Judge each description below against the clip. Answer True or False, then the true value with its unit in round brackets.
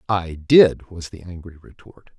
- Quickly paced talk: False (165 wpm)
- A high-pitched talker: False (90 Hz)